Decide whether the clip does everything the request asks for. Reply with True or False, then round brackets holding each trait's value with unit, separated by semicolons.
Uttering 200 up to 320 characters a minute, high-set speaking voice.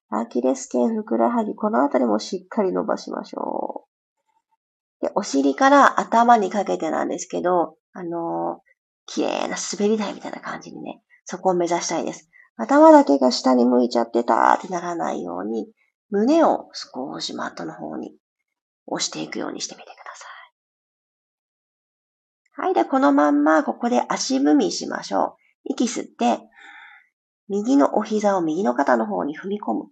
True (315 characters per minute; 195 Hz)